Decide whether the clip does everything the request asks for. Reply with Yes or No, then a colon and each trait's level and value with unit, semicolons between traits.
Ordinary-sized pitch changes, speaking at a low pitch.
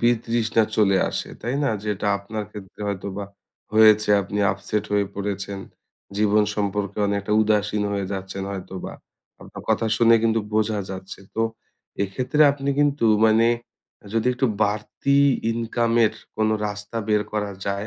No: narrow, 2.2 semitones; low, 105 Hz